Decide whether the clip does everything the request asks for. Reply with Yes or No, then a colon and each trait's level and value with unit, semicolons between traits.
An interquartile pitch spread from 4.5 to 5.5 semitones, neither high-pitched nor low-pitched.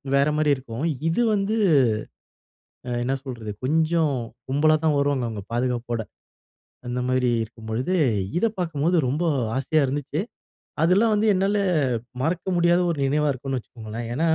Yes: average, 5.0 semitones; medium, 145 Hz